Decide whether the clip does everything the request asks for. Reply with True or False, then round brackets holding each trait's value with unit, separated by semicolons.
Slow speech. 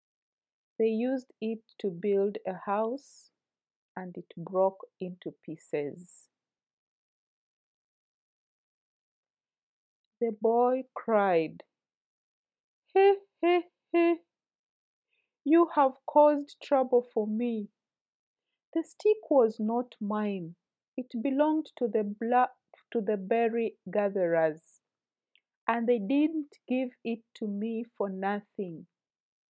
True (95 wpm)